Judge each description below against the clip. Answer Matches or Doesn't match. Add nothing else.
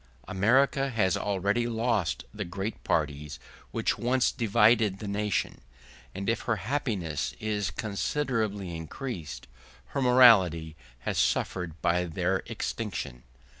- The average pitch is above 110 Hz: Doesn't match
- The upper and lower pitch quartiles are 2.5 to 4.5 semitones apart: Doesn't match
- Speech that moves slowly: Matches